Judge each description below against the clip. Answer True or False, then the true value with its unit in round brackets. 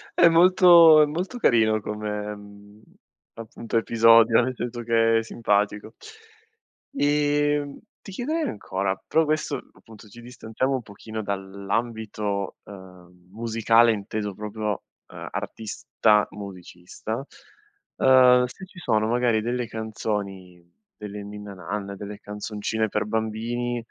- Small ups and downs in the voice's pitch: False (3.0 semitones)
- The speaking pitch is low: True (110 Hz)